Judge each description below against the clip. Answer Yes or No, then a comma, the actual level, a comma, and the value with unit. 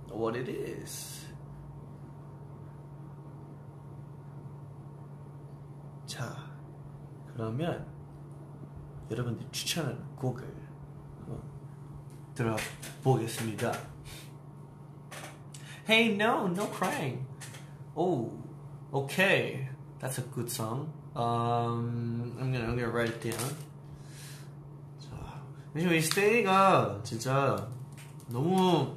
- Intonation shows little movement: Yes, narrow, 1.8 semitones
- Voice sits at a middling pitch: Yes, medium, 145 Hz